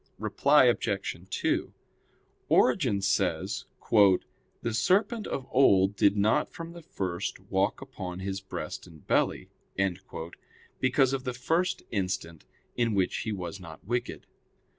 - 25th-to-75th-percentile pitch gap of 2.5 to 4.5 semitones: No, wide, 5.5 semitones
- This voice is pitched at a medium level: No, low, 100 Hz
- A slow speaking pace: Yes, slow, 125 wpm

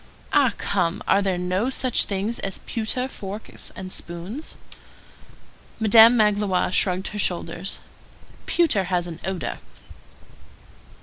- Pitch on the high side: Yes, high, 195 Hz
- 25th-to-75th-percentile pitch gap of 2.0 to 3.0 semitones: No, average, 3.5 semitones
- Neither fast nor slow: No, slow, 115 wpm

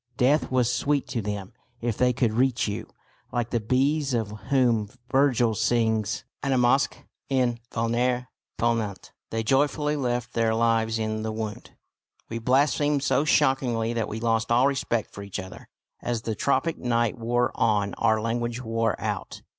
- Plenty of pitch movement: No, narrow, 2.4 semitones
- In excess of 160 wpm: No, average, 155 wpm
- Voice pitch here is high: No, low, 120 Hz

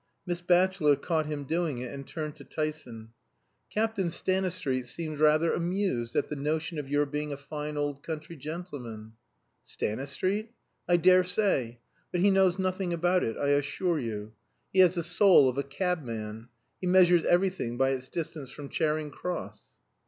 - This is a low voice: No, medium, 155 Hz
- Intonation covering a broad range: No, average, 4.5 semitones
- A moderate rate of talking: Yes, average, 160 wpm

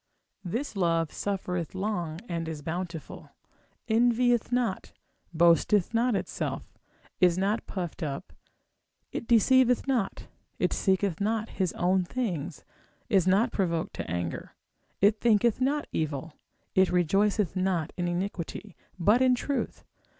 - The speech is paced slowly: Yes, slow, 125 wpm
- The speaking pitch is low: No, high, 190 Hz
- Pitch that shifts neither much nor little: Yes, average, 4.8 semitones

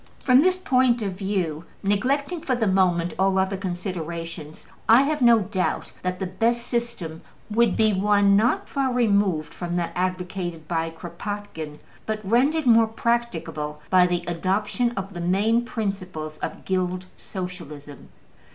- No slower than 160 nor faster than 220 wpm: No, average, 145 wpm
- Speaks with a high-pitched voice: Yes, high, 195 Hz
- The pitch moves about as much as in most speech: Yes, average, 4.8 semitones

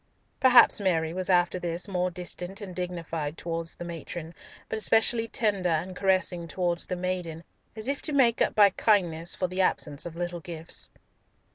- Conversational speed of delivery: Yes, average, 170 wpm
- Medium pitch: Yes, medium, 180 Hz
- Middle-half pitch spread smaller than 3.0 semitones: Yes, narrow, 2.5 semitones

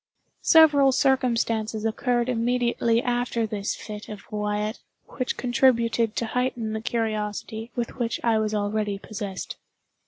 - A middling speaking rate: No, slow, 125 wpm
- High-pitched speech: Yes, high, 230 Hz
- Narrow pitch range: Yes, narrow, 2.3 semitones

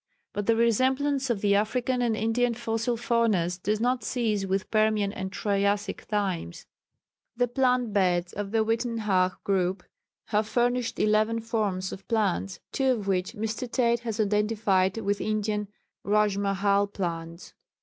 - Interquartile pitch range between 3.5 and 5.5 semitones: No, average, 2.8 semitones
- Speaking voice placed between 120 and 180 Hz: No, high, 215 Hz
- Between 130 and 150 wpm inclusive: Yes, average, 140 wpm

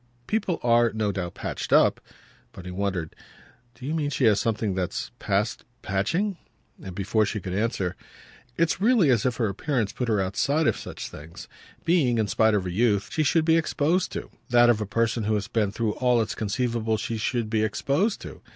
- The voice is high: No, low, 110 Hz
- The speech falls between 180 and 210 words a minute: Yes, average, 185 wpm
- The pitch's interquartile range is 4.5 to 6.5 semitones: Yes, wide, 5.4 semitones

